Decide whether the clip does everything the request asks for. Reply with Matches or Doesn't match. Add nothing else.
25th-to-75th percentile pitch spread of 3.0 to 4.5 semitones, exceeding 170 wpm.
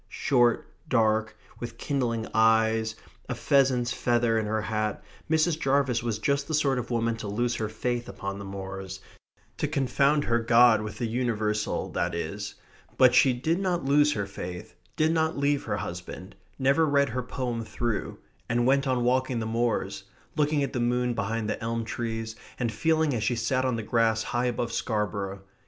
Matches